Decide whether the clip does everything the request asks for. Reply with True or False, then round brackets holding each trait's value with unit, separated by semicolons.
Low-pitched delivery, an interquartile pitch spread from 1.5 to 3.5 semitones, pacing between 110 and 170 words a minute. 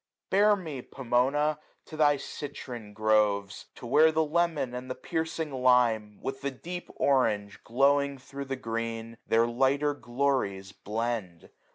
False (130 Hz; 4.3 semitones; 145 wpm)